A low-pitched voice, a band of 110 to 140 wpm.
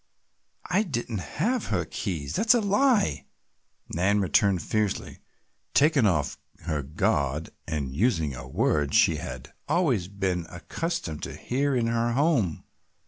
Yes: low, 100 Hz; slow, 135 wpm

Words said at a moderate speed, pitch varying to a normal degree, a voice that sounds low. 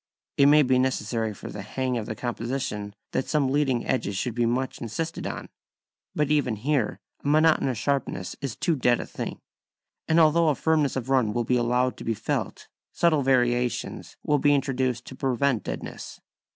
Yes: average, 180 wpm; average, 3.2 semitones; low, 130 Hz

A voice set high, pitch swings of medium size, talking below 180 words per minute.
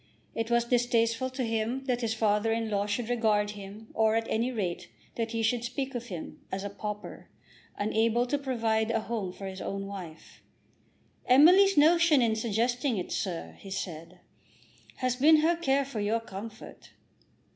Yes: high, 225 Hz; average, 3.1 semitones; average, 170 wpm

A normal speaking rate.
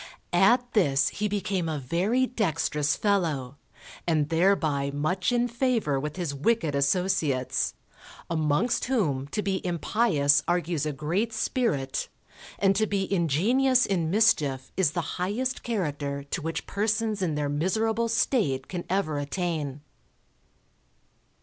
No: slow, 130 wpm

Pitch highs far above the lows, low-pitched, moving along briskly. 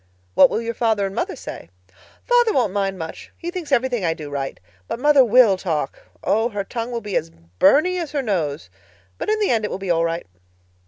No: wide, 6.8 semitones; high, 215 Hz; fast, 220 wpm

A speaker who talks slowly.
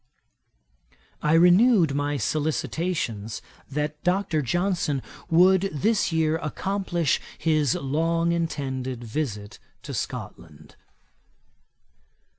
Yes: slow, 80 wpm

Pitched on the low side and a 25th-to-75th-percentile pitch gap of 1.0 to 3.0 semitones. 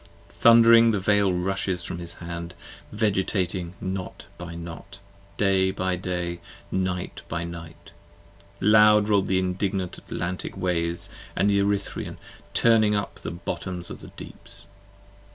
Yes: very low, 95 Hz; narrow, 2.6 semitones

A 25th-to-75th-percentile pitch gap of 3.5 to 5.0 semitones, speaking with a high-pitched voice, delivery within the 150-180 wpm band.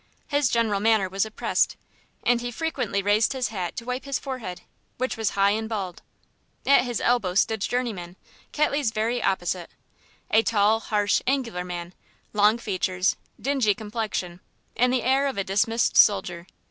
Yes: average, 3.9 semitones; high, 220 Hz; average, 160 wpm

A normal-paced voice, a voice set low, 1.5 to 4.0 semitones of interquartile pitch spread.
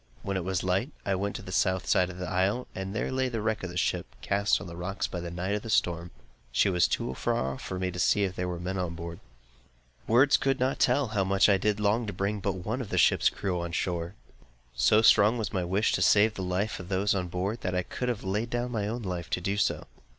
No: fast, 270 wpm; very low, 95 Hz; average, 2.9 semitones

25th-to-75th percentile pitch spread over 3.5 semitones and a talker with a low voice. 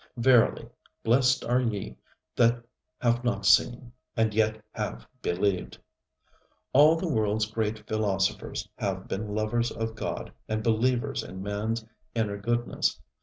No: narrow, 2.4 semitones; low, 110 Hz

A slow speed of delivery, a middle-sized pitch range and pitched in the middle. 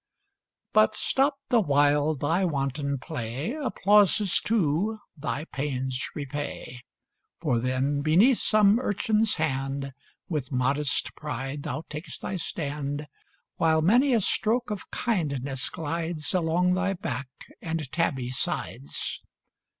No: slow, 115 wpm; wide, 5.7 semitones; medium, 155 Hz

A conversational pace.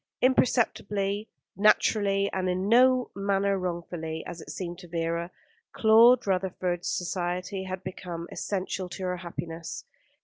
No: slow, 125 wpm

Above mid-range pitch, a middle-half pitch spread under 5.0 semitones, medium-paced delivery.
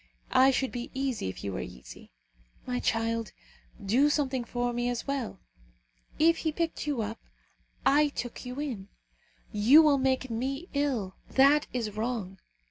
Yes: very high, 250 Hz; average, 3.7 semitones; average, 155 wpm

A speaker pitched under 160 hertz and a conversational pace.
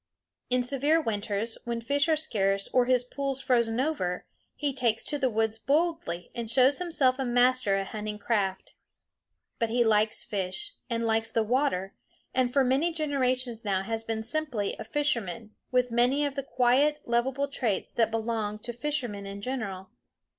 No: high, 240 Hz; average, 170 wpm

